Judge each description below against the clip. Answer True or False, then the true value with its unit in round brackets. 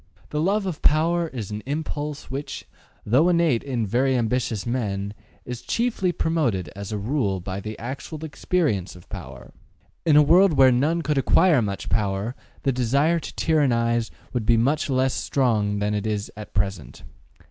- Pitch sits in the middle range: False (125 Hz)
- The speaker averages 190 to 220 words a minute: False (170 wpm)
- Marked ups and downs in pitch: True (6.4 semitones)